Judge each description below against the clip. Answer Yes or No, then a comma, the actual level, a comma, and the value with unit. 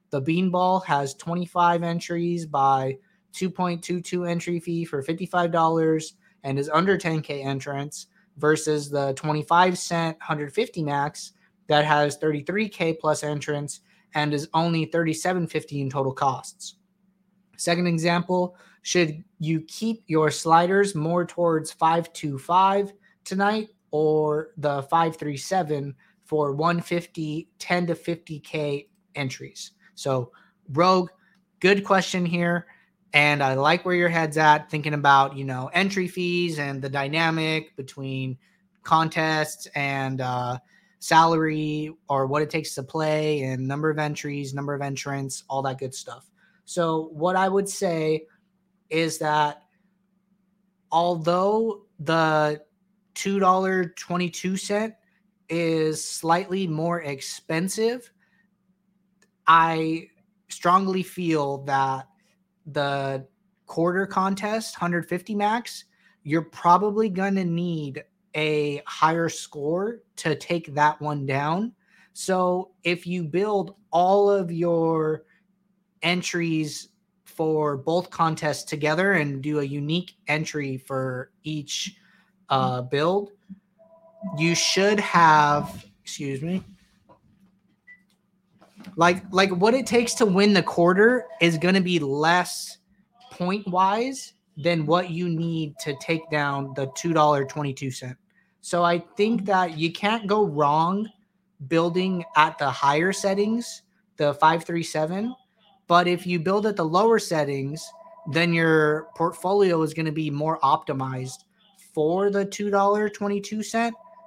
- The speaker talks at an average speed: No, slow, 115 wpm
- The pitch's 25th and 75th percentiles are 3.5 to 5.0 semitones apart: Yes, average, 4.1 semitones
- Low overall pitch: No, medium, 170 Hz